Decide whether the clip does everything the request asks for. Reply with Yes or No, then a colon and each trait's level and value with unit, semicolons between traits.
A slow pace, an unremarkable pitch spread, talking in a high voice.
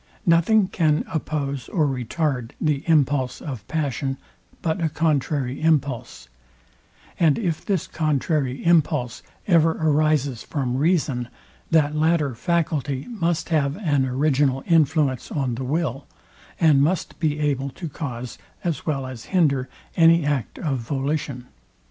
No: slow, 130 wpm; average, 3.2 semitones; medium, 150 Hz